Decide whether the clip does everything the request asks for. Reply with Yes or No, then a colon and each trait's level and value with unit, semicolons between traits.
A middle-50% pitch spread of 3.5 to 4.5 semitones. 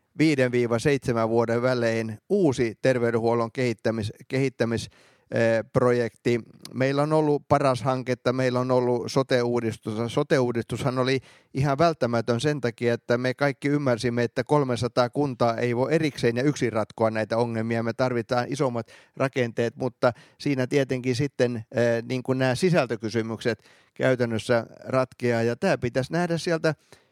No: narrow, 2.5 semitones